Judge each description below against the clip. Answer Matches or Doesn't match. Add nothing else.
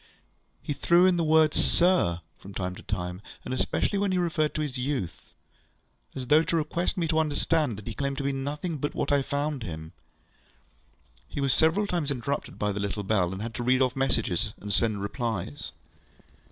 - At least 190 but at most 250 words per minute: Matches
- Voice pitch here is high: Doesn't match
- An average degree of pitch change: Doesn't match